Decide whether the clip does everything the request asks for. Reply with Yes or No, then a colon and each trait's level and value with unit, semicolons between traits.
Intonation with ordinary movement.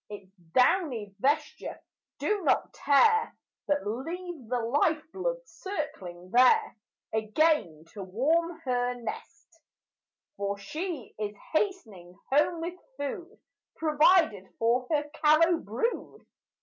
No: wide, 7.5 semitones